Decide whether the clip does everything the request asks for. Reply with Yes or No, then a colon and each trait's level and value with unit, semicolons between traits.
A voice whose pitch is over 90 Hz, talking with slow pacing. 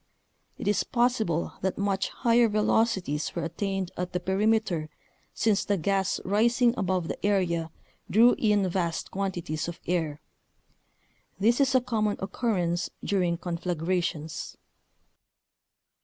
Yes: high, 190 Hz; slow, 120 wpm